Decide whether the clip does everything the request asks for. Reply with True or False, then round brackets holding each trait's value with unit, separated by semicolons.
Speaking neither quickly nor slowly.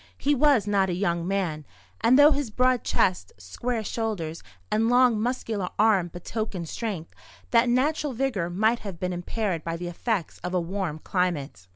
True (170 wpm)